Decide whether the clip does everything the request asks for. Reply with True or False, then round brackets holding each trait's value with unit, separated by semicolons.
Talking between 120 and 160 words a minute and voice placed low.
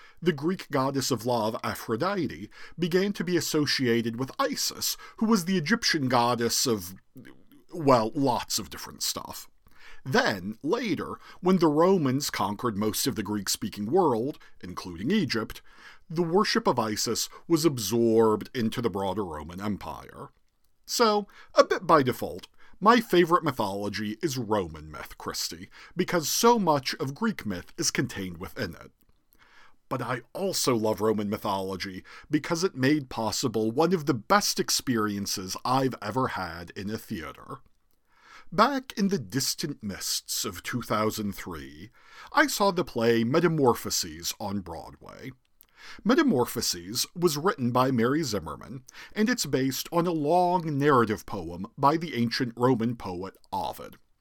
True (140 wpm; 130 Hz)